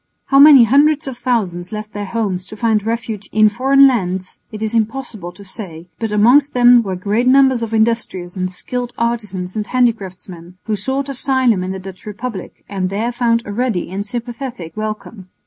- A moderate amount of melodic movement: Yes, average, 4.2 semitones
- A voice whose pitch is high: Yes, high, 220 Hz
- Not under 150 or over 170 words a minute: No, average, 180 wpm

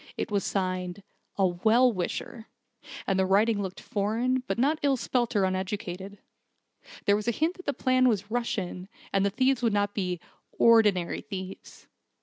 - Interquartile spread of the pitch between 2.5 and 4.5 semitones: Yes, average, 4.0 semitones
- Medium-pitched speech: No, high, 205 Hz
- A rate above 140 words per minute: Yes, average, 165 wpm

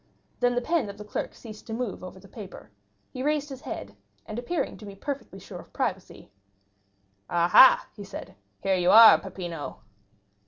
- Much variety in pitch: No, average, 4.8 semitones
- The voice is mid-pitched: No, high, 210 Hz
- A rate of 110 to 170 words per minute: No, average, 185 wpm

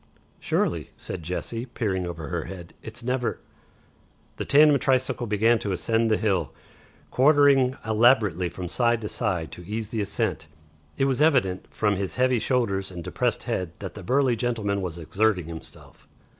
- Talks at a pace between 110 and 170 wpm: Yes, average, 165 wpm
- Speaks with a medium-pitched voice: No, low, 110 Hz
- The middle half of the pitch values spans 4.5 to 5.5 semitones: Yes, average, 5.2 semitones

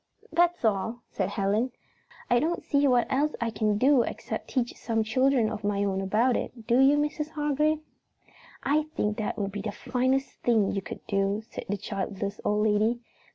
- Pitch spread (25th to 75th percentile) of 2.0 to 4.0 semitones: No, average, 4.6 semitones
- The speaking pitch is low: No, high, 230 Hz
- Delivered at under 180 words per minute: No, average, 185 wpm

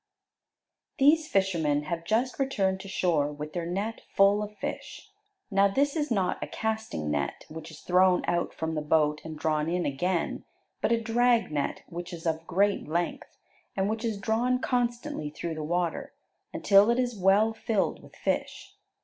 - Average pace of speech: Yes, average, 175 wpm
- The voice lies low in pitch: No, high, 190 Hz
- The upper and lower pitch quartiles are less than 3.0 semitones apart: No, wide, 5.6 semitones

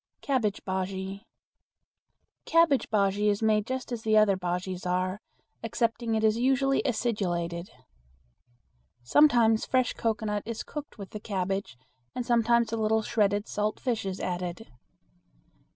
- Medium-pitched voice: No, high, 215 Hz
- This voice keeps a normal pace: No, slow, 125 wpm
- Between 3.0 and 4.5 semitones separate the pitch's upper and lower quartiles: Yes, average, 3.4 semitones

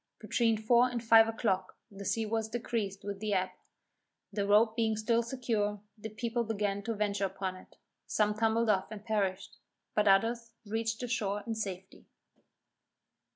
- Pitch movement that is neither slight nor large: No, narrow, 2.1 semitones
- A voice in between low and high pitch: No, high, 215 Hz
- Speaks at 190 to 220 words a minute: No, average, 160 wpm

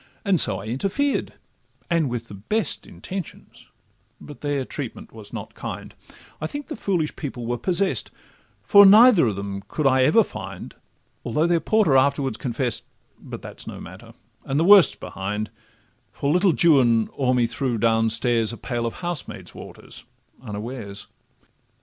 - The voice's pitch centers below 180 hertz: Yes, low, 135 Hz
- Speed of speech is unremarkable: Yes, average, 160 wpm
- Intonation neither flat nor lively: No, wide, 7.1 semitones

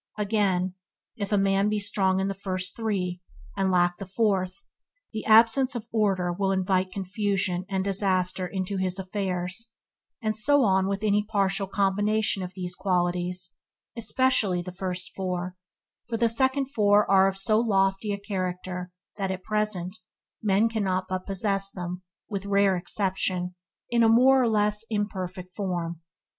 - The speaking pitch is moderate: No, high, 195 Hz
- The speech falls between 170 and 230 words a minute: No, average, 155 wpm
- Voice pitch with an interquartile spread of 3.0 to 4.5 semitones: No, narrow, 2.4 semitones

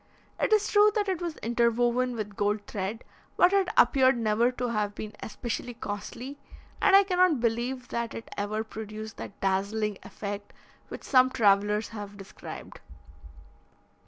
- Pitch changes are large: No, average, 3.8 semitones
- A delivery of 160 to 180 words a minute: No, average, 150 wpm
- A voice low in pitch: No, high, 230 Hz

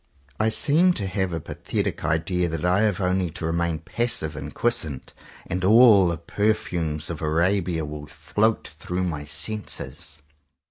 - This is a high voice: No, very low, 90 Hz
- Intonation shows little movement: No, average, 4.6 semitones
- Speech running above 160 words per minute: No, average, 150 wpm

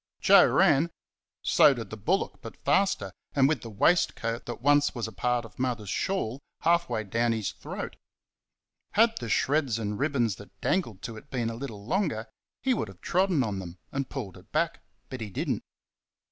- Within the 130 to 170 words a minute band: No, average, 190 wpm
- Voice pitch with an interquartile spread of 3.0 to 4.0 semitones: No, average, 4.8 semitones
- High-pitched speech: No, low, 120 Hz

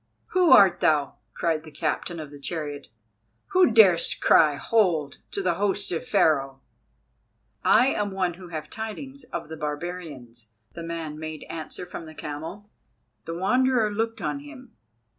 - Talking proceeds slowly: No, average, 155 wpm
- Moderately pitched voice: Yes, medium, 170 Hz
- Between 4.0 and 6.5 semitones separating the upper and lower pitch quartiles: Yes, wide, 5.4 semitones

